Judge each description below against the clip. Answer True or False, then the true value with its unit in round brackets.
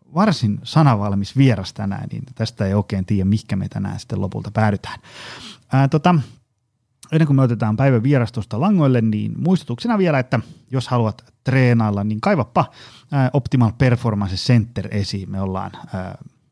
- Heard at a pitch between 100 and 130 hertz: True (120 Hz)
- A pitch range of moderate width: True (4.7 semitones)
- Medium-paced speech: True (145 wpm)